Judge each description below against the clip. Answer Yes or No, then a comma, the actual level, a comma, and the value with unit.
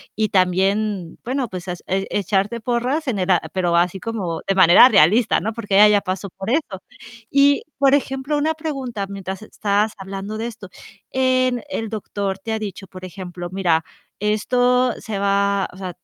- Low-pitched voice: No, high, 205 Hz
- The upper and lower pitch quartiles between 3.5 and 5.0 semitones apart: Yes, average, 4.0 semitones